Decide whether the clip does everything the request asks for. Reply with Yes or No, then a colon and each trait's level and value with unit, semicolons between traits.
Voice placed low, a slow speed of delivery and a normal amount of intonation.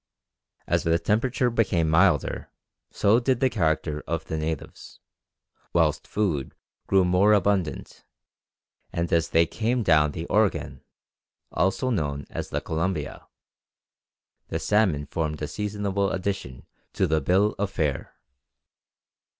Yes: very low, 90 Hz; slow, 125 wpm; average, 4.6 semitones